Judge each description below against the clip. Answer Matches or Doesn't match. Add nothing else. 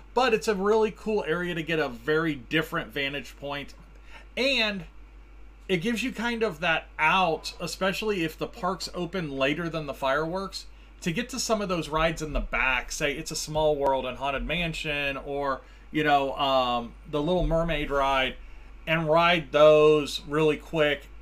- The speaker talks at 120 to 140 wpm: Doesn't match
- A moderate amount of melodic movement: Matches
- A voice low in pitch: Doesn't match